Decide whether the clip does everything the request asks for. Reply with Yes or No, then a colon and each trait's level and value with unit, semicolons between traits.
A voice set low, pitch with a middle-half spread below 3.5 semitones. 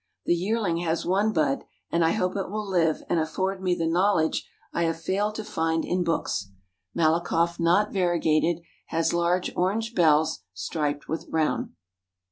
No: medium, 170 Hz; narrow, 2.6 semitones